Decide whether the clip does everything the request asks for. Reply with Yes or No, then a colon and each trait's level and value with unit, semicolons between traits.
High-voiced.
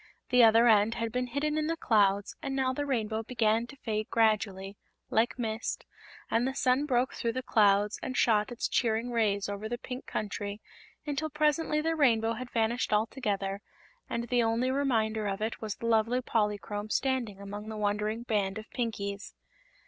Yes: high, 225 Hz